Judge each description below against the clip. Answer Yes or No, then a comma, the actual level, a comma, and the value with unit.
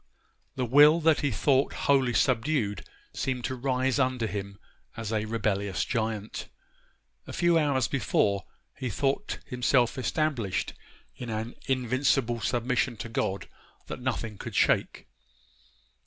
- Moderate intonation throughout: Yes, average, 3.4 semitones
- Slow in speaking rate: Yes, slow, 125 wpm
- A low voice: Yes, low, 125 Hz